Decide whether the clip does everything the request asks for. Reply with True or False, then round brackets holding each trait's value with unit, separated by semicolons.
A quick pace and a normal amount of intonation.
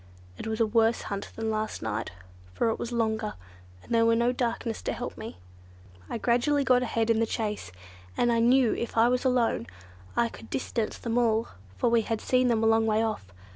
False (210 wpm; 1.4 semitones)